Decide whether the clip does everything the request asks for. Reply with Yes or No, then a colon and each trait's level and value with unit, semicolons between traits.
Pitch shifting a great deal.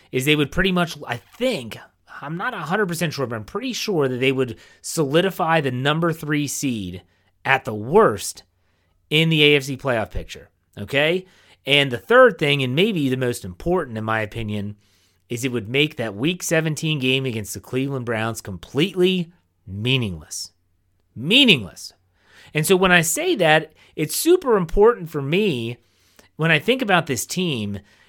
Yes: wide, 7.9 semitones